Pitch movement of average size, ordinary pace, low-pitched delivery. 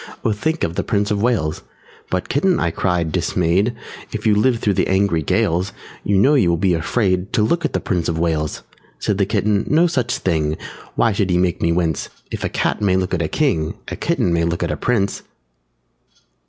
No: average, 4.2 semitones; fast, 220 wpm; very low, 95 Hz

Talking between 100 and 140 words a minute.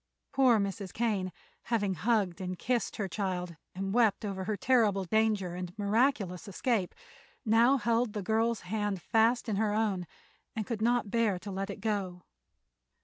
No: average, 160 wpm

